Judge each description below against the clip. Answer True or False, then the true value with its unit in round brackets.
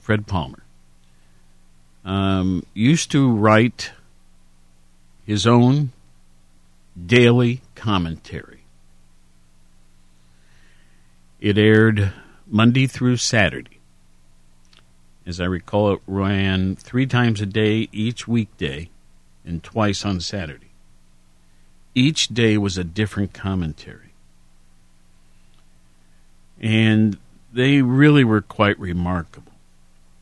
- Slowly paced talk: True (85 wpm)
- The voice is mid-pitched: False (85 Hz)